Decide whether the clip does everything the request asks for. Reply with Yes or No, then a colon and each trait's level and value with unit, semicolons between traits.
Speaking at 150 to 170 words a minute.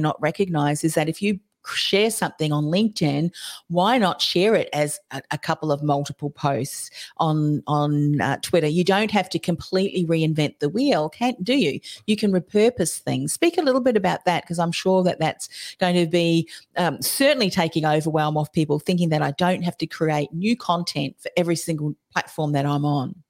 No: average, 195 wpm